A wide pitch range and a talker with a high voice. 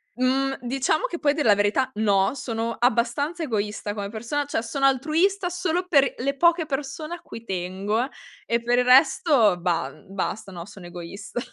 Yes: wide, 6.0 semitones; high, 245 Hz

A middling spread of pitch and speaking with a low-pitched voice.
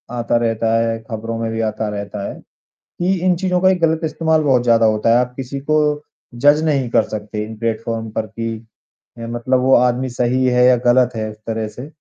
Yes: average, 3.0 semitones; low, 120 Hz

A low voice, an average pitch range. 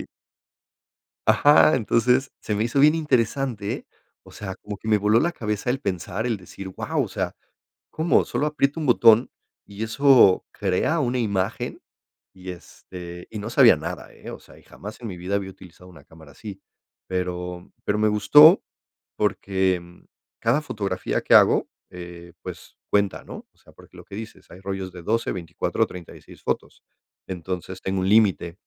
Yes: low, 100 Hz; average, 4.2 semitones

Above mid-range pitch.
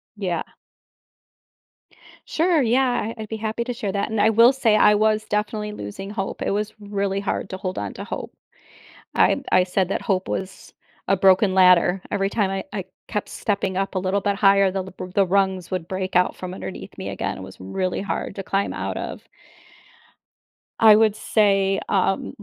Yes: high, 195 Hz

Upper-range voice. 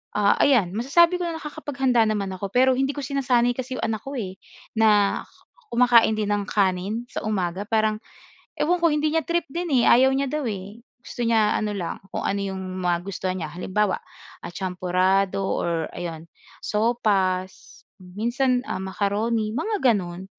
Yes: high, 215 Hz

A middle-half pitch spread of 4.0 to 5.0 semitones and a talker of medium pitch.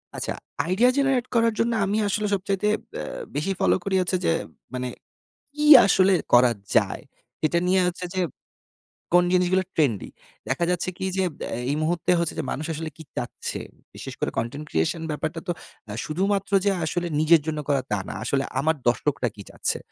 Yes: average, 4.5 semitones; medium, 175 Hz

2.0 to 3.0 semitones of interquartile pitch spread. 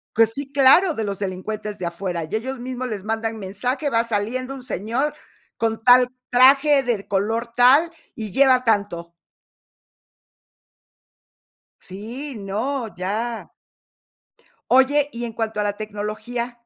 No: average, 3.8 semitones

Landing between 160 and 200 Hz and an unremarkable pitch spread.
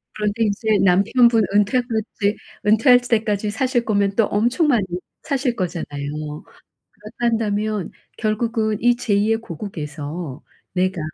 No: high, 210 Hz; average, 3.4 semitones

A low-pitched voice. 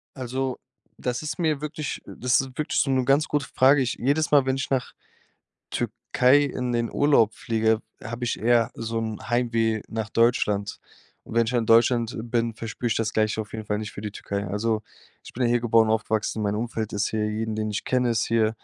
Yes: low, 115 Hz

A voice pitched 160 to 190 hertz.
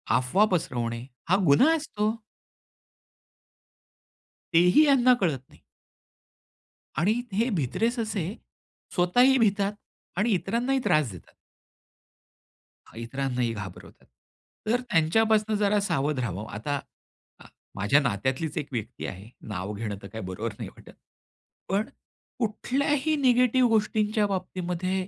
Yes: medium, 185 Hz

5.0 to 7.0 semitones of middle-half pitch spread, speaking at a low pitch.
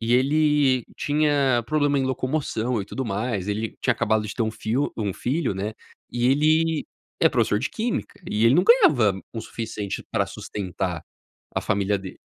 Yes: wide, 5.6 semitones; low, 120 Hz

